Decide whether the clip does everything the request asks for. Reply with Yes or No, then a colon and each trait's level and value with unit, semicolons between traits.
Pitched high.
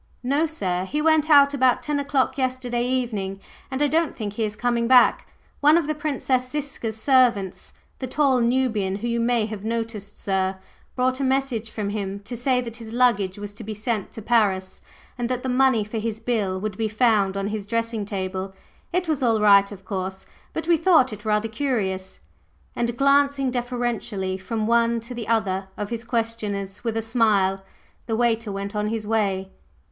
Yes: high, 230 Hz